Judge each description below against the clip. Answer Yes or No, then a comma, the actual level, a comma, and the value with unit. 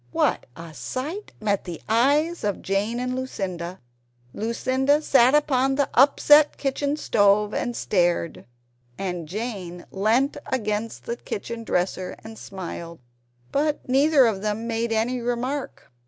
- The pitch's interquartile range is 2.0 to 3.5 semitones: No, average, 5.2 semitones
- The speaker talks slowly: Yes, slow, 130 wpm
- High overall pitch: Yes, high, 230 Hz